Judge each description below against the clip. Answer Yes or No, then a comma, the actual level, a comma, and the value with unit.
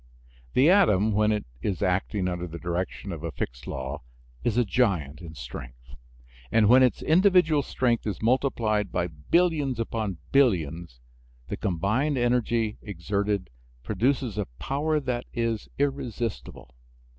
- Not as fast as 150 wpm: Yes, slow, 135 wpm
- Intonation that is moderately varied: No, wide, 6.4 semitones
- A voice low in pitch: Yes, low, 105 Hz